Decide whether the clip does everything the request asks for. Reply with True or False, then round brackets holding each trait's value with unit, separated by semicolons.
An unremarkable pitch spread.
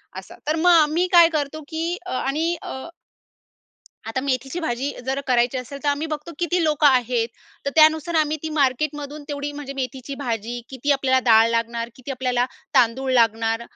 True (3.8 semitones)